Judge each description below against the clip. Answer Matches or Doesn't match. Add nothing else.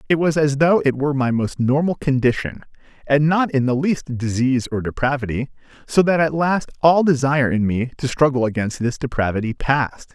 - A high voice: Doesn't match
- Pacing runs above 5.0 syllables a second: Matches